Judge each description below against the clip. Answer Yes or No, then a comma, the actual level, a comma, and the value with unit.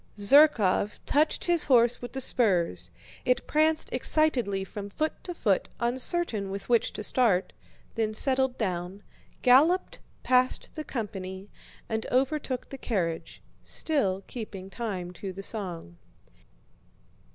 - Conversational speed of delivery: No, slow, 125 wpm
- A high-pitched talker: Yes, high, 225 Hz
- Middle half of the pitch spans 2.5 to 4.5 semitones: No, wide, 5.4 semitones